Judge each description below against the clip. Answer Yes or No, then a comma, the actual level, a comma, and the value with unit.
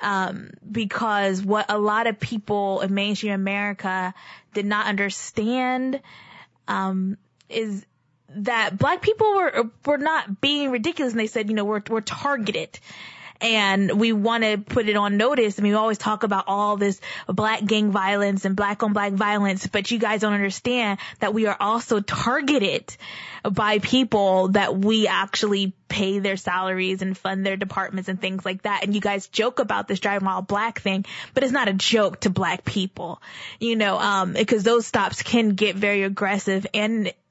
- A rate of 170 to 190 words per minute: Yes, average, 180 wpm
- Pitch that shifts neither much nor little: No, narrow, 2.3 semitones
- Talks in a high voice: Yes, high, 205 Hz